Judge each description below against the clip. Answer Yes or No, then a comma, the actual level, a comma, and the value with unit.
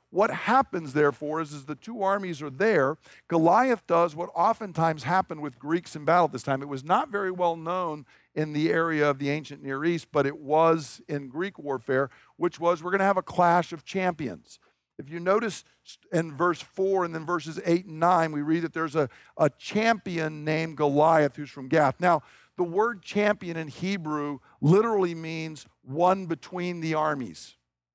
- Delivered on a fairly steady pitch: No, average, 3.3 semitones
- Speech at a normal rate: Yes, average, 190 wpm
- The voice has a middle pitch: Yes, medium, 165 Hz